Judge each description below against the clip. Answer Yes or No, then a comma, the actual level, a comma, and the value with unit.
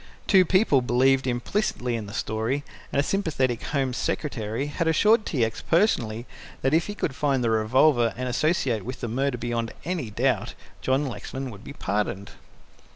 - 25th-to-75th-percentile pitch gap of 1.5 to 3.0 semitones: No, average, 4.3 semitones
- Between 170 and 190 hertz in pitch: No, low, 130 Hz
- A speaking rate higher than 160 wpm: Yes, average, 175 wpm